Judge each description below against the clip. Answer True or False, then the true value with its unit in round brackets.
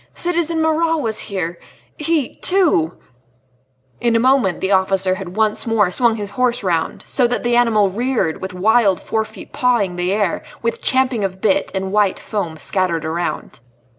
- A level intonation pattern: False (4.9 semitones)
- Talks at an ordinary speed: True (165 wpm)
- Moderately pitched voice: False (205 Hz)